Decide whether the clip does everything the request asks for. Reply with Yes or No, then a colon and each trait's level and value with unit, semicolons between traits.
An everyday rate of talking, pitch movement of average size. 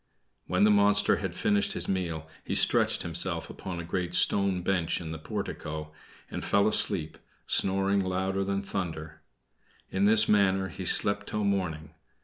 Yes: average, 155 wpm; average, 3.0 semitones